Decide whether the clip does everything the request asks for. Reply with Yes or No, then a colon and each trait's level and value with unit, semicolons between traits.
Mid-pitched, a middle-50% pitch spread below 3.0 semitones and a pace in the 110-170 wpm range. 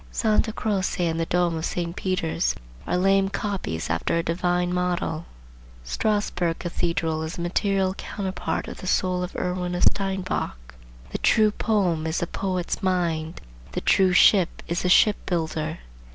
Yes: medium, 180 Hz; narrow, 2.5 semitones; average, 155 wpm